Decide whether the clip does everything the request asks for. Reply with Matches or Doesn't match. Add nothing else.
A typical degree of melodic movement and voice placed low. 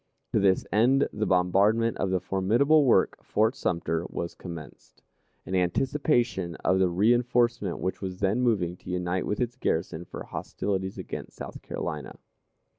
Matches